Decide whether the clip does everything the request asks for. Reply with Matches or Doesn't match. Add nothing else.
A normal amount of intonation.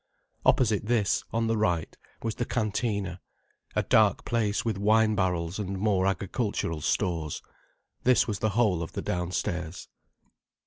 Matches